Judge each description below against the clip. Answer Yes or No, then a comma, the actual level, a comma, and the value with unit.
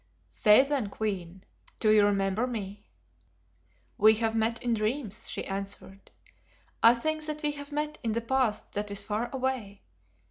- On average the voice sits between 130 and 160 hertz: No, high, 220 Hz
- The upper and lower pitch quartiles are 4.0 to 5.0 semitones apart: Yes, average, 4.3 semitones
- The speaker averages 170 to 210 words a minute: No, average, 155 wpm